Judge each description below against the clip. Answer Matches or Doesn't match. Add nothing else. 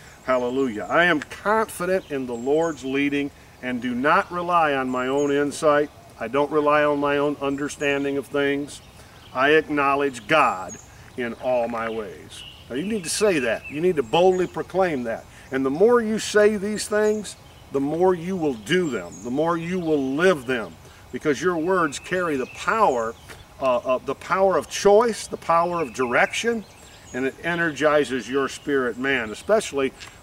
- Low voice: Doesn't match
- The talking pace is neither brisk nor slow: Matches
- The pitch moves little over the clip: Doesn't match